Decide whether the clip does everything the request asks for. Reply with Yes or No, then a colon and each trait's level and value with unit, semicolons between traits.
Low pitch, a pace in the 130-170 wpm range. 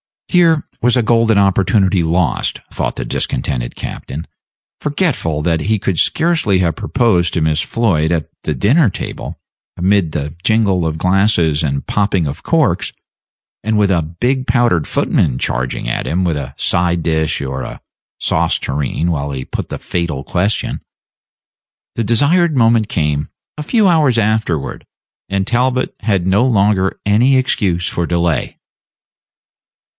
Yes: very low, 95 Hz; average, 145 wpm